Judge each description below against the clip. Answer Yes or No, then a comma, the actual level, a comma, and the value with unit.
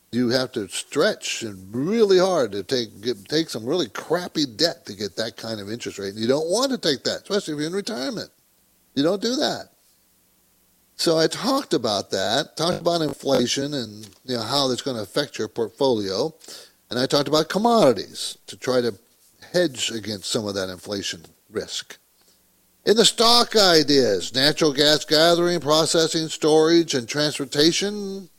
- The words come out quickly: No, average, 175 wpm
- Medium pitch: Yes, medium, 150 Hz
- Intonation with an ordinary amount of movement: No, wide, 6.4 semitones